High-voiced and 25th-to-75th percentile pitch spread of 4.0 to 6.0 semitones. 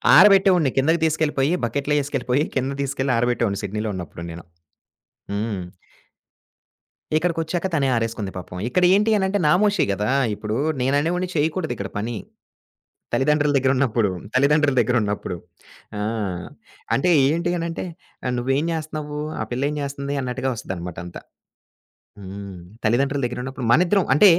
No: low, 135 Hz; wide, 5.4 semitones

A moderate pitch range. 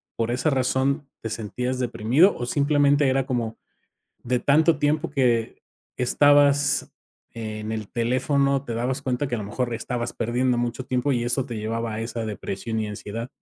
Yes: average, 3.3 semitones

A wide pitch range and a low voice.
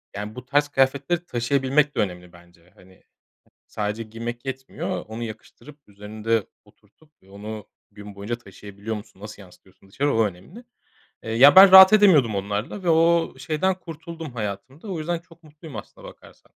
Yes: wide, 7.0 semitones; low, 120 Hz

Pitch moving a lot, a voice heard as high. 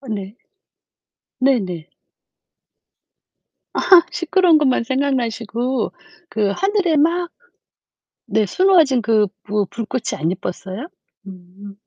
Yes: wide, 7.1 semitones; high, 235 Hz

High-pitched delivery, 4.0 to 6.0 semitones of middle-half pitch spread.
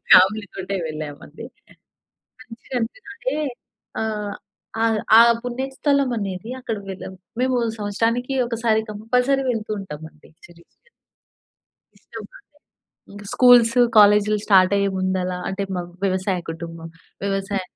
Yes: high, 210 Hz; average, 4.6 semitones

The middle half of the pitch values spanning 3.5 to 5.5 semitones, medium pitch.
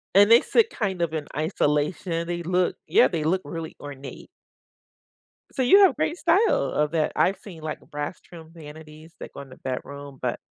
Yes: average, 4.0 semitones; medium, 165 Hz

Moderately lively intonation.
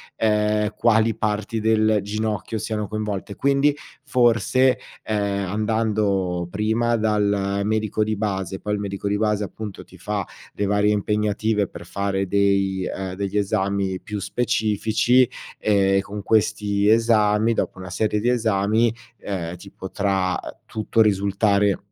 No: narrow, 1.7 semitones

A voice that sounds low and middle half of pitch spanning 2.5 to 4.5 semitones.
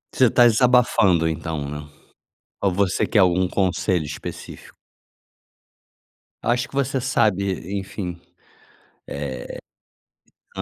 No: very low, 95 Hz; wide, 5.5 semitones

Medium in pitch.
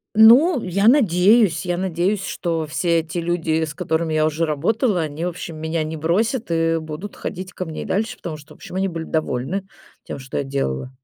Yes: medium, 170 Hz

